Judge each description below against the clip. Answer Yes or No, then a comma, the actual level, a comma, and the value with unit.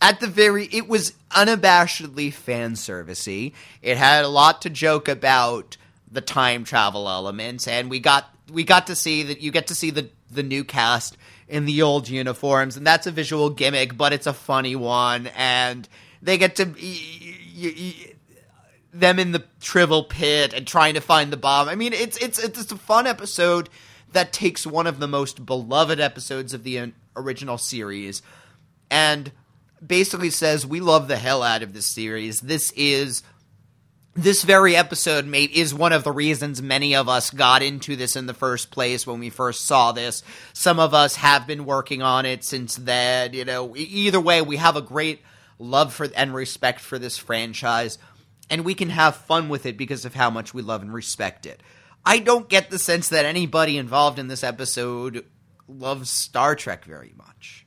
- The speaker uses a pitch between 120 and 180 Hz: Yes, medium, 140 Hz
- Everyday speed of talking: Yes, average, 190 wpm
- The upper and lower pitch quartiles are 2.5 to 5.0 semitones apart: Yes, average, 4.5 semitones